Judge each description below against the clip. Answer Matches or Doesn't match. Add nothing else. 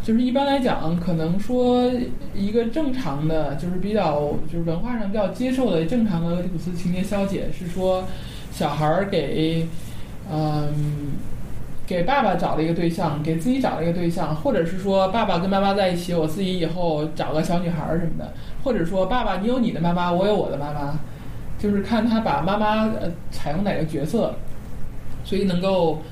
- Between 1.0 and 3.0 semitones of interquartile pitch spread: Doesn't match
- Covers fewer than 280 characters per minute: Doesn't match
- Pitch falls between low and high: Matches